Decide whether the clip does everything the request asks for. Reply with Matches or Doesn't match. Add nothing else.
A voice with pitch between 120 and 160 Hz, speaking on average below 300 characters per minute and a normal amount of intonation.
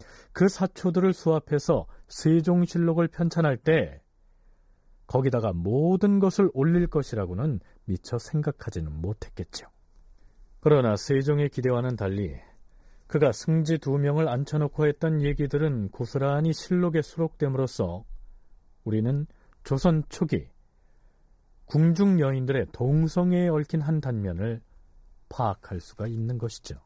Doesn't match